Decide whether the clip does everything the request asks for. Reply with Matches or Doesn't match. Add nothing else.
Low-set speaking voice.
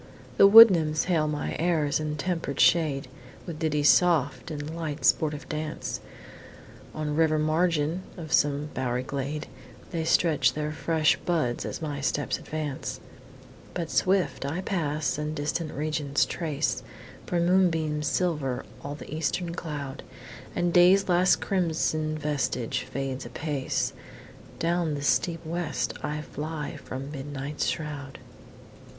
Doesn't match